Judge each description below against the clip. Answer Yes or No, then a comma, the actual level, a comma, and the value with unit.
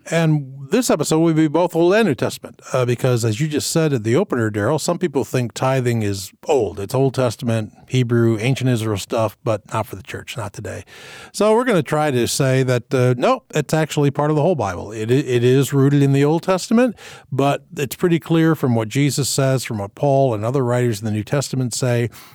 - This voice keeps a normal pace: No, fast, 225 wpm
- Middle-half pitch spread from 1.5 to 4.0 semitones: No, average, 4.5 semitones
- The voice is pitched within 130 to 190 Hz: Yes, low, 135 Hz